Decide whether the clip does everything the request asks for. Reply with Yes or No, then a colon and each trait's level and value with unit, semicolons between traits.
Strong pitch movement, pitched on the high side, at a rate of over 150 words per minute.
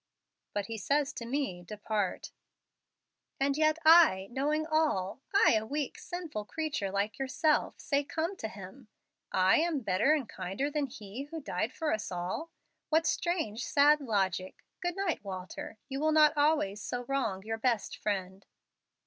Yes: wide, 7.2 semitones; very high, 265 Hz; average, 160 wpm